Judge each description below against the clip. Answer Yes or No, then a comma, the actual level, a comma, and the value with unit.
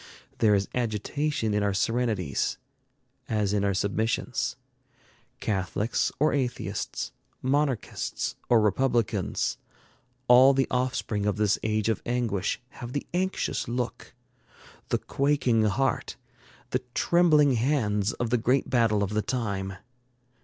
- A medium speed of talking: No, slow, 120 wpm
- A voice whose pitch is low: Yes, low, 115 Hz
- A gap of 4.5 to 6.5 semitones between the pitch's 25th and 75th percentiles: No, average, 3.9 semitones